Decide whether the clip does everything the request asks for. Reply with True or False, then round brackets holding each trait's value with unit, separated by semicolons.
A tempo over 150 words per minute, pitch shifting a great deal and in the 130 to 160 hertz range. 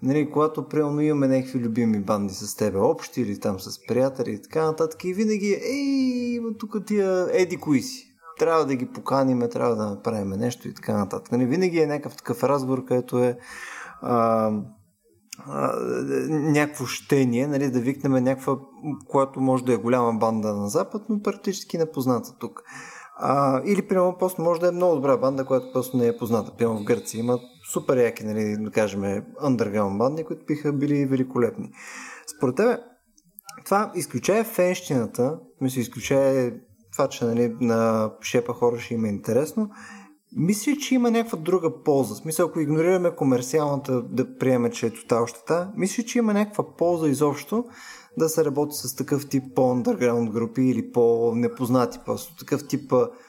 True (160 wpm; 6.6 semitones; 135 Hz)